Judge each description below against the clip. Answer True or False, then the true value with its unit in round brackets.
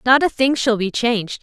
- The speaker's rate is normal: False (250 wpm)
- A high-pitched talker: True (240 Hz)